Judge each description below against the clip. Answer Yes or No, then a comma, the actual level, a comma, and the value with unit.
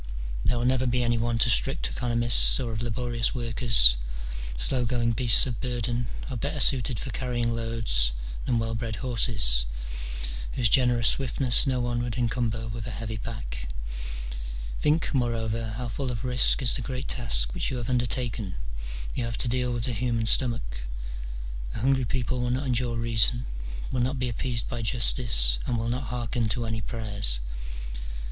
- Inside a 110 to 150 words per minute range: No, average, 170 wpm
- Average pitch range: No, narrow, 1.8 semitones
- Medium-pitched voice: No, low, 120 Hz